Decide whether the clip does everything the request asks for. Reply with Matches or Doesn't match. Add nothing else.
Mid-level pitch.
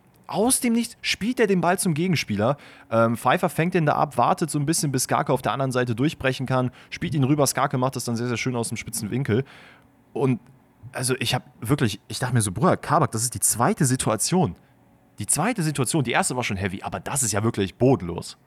Doesn't match